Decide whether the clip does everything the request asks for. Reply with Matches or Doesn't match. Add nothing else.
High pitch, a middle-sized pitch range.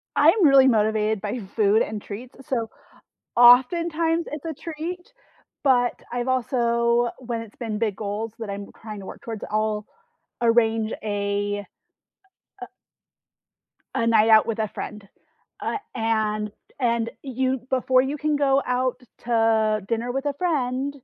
Matches